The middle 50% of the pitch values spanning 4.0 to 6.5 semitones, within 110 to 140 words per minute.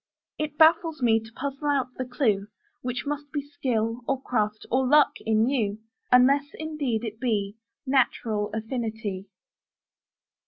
Yes: average, 4.3 semitones; slow, 135 wpm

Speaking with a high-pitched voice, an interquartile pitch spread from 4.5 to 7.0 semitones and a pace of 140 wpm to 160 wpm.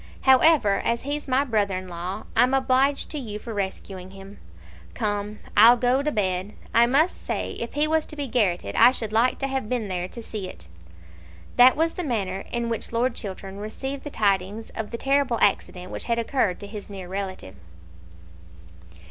No: high, 225 Hz; average, 5.0 semitones; average, 190 wpm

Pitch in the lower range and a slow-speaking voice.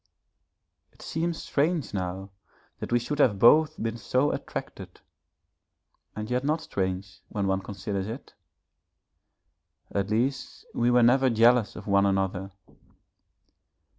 Yes: low, 115 Hz; slow, 125 wpm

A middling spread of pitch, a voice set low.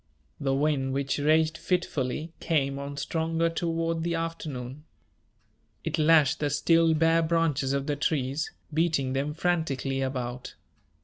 No: average, 3.2 semitones; medium, 150 Hz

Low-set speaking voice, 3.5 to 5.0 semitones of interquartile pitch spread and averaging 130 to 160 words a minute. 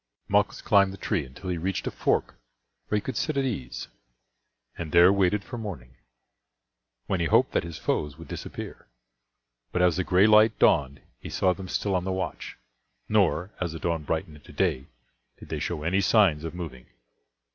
No: very low, 90 Hz; average, 4.0 semitones; average, 190 wpm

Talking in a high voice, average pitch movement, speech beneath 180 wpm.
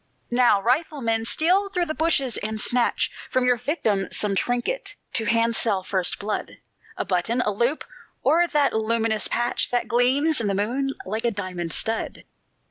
Yes: high, 235 Hz; average, 4.3 semitones; average, 160 wpm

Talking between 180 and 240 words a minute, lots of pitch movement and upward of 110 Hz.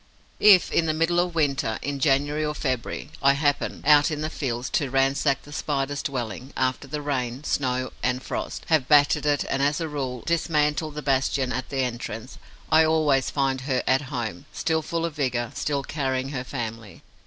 No: average, 190 wpm; average, 2.7 semitones; medium, 140 Hz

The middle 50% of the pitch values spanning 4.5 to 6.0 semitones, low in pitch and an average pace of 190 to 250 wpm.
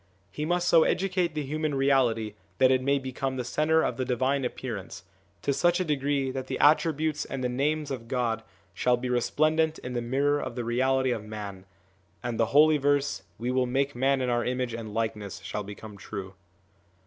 No: average, 3.4 semitones; low, 130 Hz; average, 200 wpm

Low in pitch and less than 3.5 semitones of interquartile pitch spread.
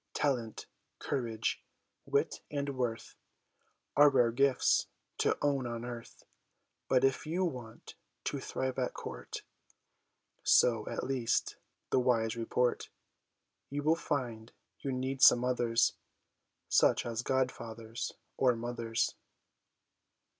Yes: low, 125 Hz; narrow, 2.6 semitones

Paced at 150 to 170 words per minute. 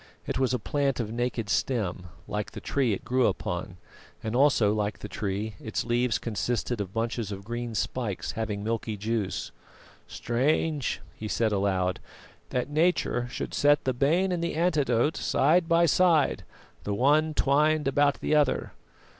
Yes: average, 165 wpm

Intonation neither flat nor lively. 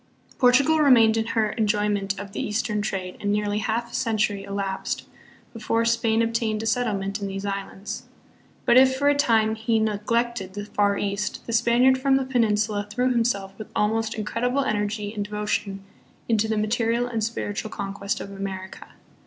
No: narrow, 2.2 semitones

